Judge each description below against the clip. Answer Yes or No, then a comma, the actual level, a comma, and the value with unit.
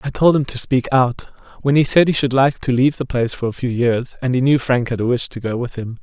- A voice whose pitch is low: Yes, low, 130 Hz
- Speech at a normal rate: No, fast, 310 wpm